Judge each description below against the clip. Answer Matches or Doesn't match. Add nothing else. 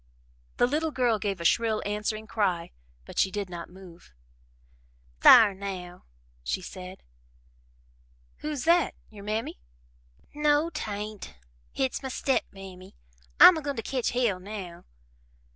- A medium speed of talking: Doesn't match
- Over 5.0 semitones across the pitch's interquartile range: Matches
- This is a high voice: Matches